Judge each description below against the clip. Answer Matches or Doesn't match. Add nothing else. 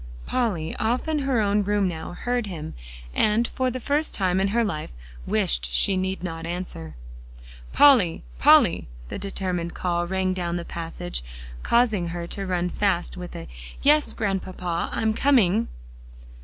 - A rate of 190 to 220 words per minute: Doesn't match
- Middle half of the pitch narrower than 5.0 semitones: Matches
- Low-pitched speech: Doesn't match